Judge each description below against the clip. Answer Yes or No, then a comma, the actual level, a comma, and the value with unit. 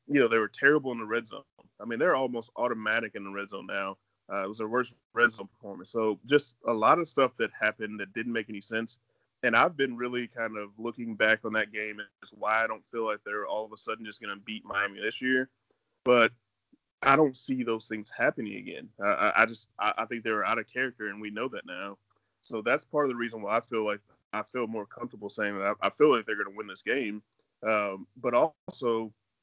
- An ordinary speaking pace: No, fast, 245 wpm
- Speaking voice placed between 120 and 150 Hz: No, low, 110 Hz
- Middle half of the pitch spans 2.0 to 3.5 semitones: Yes, narrow, 2.6 semitones